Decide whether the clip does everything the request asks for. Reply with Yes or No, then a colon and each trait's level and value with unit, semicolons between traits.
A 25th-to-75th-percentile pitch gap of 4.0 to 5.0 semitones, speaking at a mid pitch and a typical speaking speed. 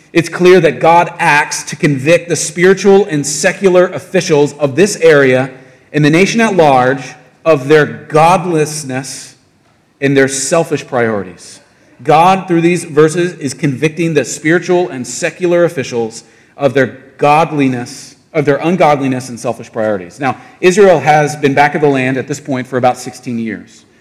Yes: average, 4.7 semitones; medium, 145 Hz; average, 155 wpm